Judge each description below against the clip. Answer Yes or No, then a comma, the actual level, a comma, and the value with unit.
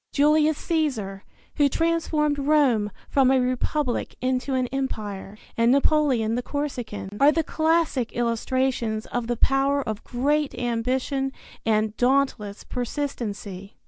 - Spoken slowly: Yes, slow, 120 wpm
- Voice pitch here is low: No, very high, 260 Hz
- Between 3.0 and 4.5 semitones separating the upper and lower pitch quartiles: Yes, average, 4.1 semitones